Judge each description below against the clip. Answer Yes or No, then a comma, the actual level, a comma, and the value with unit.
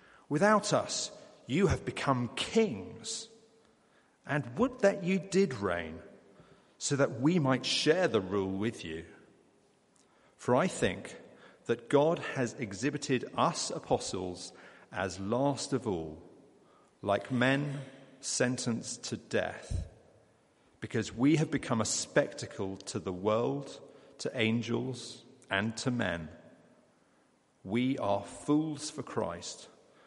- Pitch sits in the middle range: No, low, 125 Hz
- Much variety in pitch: Yes, wide, 6.1 semitones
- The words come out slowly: Yes, slow, 115 wpm